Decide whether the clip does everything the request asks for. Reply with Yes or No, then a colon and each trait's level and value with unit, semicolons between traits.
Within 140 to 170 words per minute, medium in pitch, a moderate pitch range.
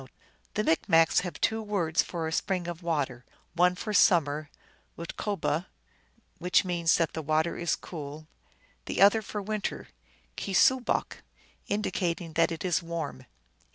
Yes: average, 145 wpm; medium, 170 Hz; average, 3.3 semitones